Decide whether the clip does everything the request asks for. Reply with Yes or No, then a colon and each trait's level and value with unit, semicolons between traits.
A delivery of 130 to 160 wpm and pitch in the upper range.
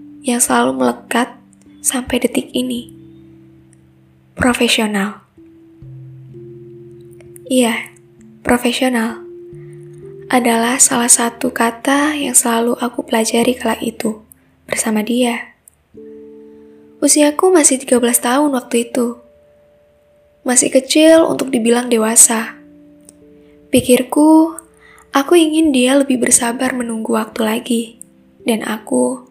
No: average, 90 wpm; high, 230 Hz